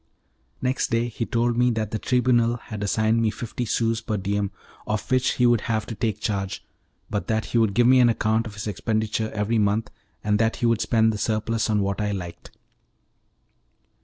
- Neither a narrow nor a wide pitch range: No, narrow, 1.9 semitones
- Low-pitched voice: Yes, low, 110 Hz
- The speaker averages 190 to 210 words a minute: Yes, average, 200 wpm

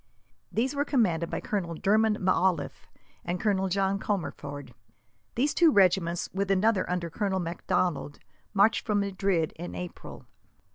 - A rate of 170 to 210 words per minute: No, slow, 135 wpm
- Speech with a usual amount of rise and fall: Yes, average, 3.2 semitones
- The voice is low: No, high, 190 Hz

